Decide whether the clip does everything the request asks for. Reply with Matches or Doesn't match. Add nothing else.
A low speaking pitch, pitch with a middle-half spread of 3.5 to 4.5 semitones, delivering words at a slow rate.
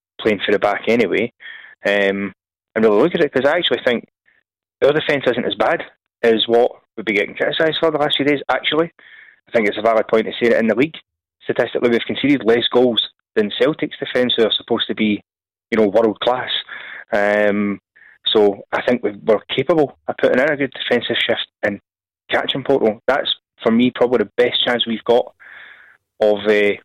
Doesn't match